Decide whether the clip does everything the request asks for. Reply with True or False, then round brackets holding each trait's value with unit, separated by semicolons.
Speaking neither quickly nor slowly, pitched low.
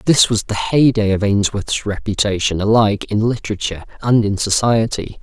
True (150 wpm; 105 Hz)